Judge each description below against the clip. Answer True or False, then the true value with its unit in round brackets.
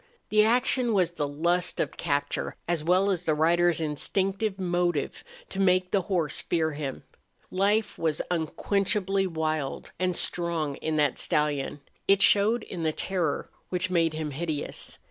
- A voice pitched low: False (175 Hz)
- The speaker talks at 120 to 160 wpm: True (150 wpm)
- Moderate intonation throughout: True (3.7 semitones)